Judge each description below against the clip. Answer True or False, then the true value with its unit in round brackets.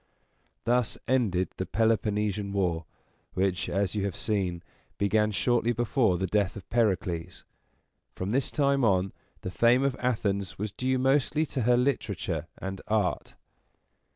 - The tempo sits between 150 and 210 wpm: False (140 wpm)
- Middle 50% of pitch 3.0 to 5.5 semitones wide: True (4.2 semitones)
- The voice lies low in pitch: True (105 Hz)